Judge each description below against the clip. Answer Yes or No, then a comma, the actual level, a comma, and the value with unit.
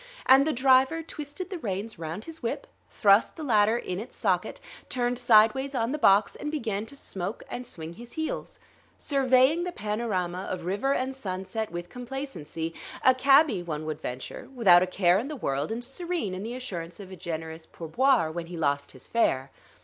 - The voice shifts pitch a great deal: Yes, wide, 7.1 semitones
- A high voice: Yes, high, 220 Hz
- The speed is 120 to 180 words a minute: No, average, 190 wpm